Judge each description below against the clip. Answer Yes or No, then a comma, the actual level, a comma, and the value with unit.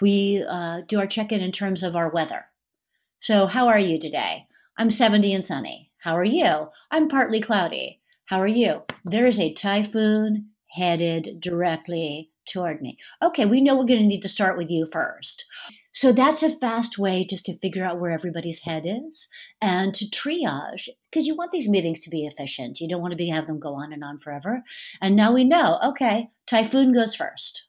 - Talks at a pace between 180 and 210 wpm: Yes, average, 200 wpm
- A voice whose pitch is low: No, high, 200 Hz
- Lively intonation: Yes, wide, 5.7 semitones